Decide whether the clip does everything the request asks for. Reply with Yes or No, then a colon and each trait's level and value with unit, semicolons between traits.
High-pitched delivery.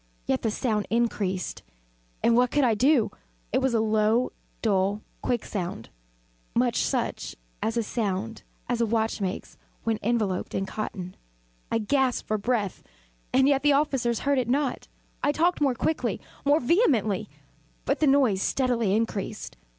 Yes: high, 230 Hz